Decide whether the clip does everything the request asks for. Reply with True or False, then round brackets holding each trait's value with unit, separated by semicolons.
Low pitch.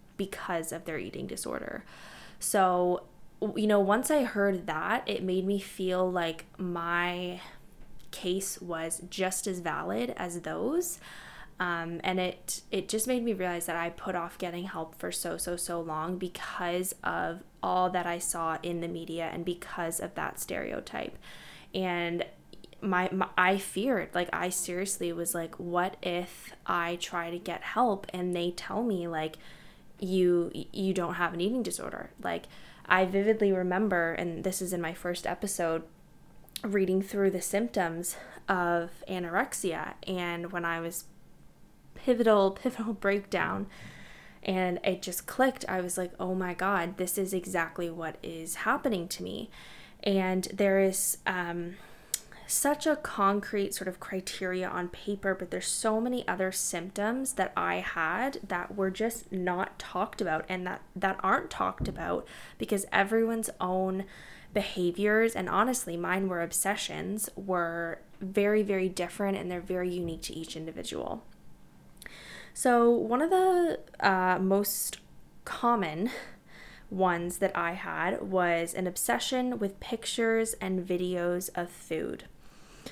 False (185 Hz)